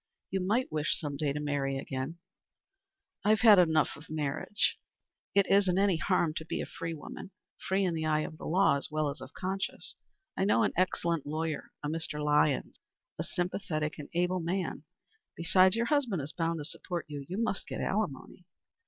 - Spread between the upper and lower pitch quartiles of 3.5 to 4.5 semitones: Yes, average, 4.0 semitones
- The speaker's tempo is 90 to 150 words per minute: No, average, 190 wpm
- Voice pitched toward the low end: No, medium, 165 Hz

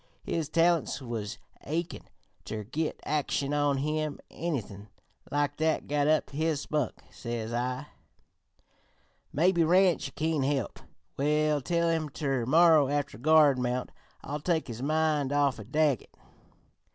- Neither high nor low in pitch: Yes, medium, 145 Hz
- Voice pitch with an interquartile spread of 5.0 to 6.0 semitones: No, average, 3.0 semitones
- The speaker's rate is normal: No, slow, 125 wpm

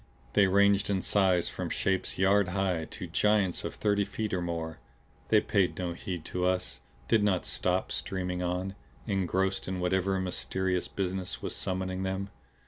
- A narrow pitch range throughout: Yes, narrow, 1.4 semitones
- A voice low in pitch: Yes, very low, 95 Hz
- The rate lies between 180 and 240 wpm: No, average, 160 wpm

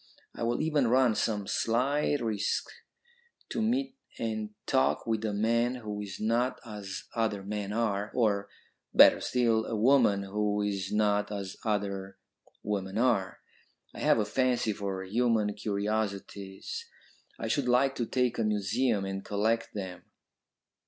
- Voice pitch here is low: Yes, low, 110 Hz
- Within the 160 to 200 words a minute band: No, average, 145 wpm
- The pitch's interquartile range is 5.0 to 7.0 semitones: No, average, 2.9 semitones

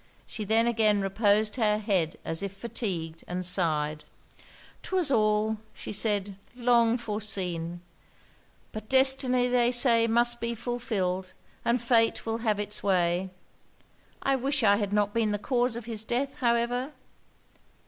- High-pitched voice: Yes, high, 220 Hz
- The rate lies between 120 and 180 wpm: Yes, average, 140 wpm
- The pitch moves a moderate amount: Yes, average, 3.2 semitones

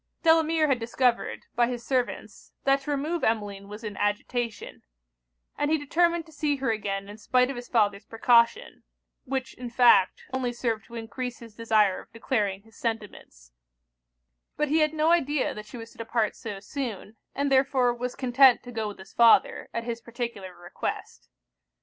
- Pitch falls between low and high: No, high, 240 Hz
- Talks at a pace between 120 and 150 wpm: No, average, 175 wpm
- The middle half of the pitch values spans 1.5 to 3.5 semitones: No, average, 3.9 semitones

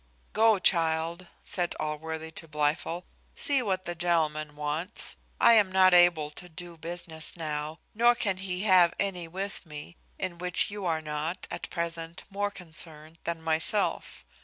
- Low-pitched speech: No, medium, 170 Hz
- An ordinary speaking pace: Yes, average, 160 wpm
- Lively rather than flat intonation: No, average, 2.8 semitones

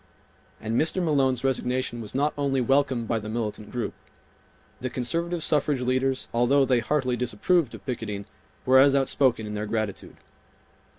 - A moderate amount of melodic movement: Yes, average, 3.3 semitones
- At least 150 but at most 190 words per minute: Yes, average, 155 wpm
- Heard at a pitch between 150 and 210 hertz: No, low, 130 Hz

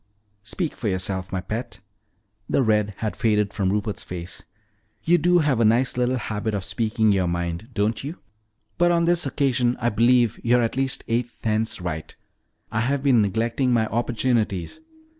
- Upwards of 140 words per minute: Yes, average, 170 wpm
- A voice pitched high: No, low, 115 Hz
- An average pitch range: Yes, average, 3.6 semitones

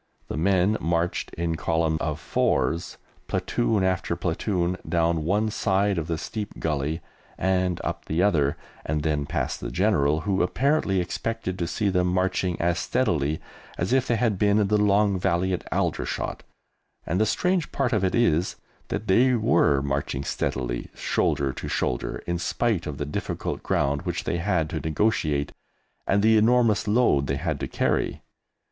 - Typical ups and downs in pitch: Yes, average, 4.8 semitones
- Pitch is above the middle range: No, very low, 90 Hz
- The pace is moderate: Yes, average, 165 wpm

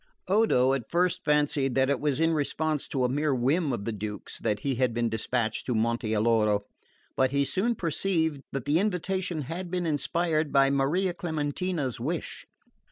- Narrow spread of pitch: No, average, 5.1 semitones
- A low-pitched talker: No, medium, 145 Hz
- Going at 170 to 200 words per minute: Yes, average, 175 wpm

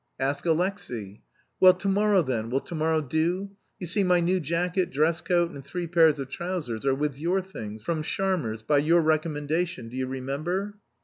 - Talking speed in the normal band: Yes, average, 185 wpm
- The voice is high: No, medium, 160 Hz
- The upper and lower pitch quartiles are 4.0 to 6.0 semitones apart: Yes, average, 4.7 semitones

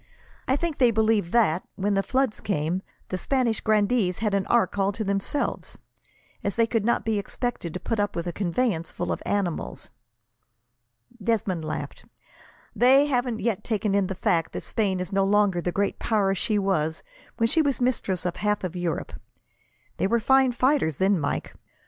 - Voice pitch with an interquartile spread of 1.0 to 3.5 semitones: No, average, 4.0 semitones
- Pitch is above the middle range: Yes, high, 205 Hz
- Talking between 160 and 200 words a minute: Yes, average, 180 wpm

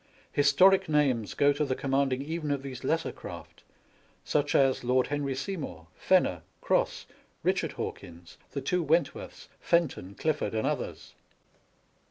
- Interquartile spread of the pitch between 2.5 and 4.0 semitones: Yes, average, 2.9 semitones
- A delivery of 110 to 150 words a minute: Yes, slow, 135 wpm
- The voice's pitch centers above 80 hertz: Yes, medium, 140 Hz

